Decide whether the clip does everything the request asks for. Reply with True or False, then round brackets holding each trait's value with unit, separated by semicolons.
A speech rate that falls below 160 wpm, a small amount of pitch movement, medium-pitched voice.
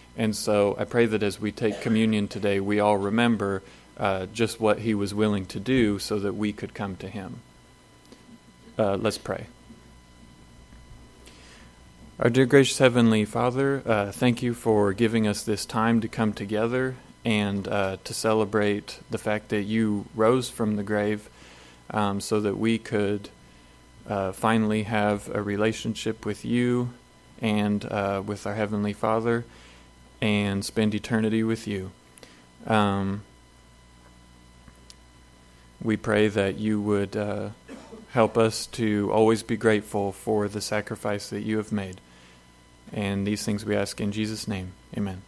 False (145 wpm; 2.1 semitones; 105 Hz)